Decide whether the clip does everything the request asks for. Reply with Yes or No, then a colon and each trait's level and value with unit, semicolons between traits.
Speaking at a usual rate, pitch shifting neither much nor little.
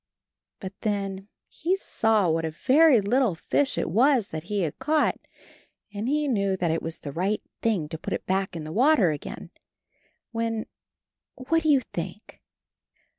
No: average, 175 wpm; wide, 7.0 semitones